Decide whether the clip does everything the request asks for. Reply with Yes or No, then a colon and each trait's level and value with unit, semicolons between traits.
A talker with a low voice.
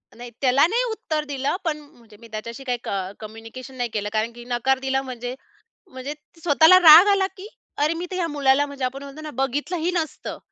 No: very high, 270 Hz